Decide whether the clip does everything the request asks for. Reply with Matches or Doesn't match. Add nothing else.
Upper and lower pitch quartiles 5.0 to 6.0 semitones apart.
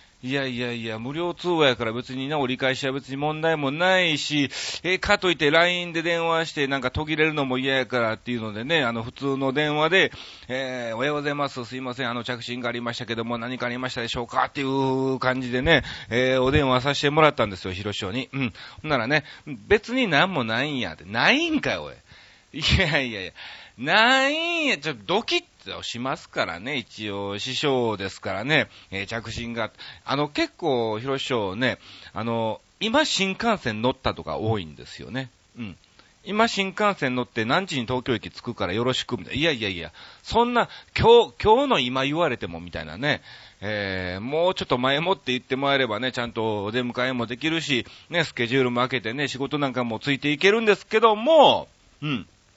Matches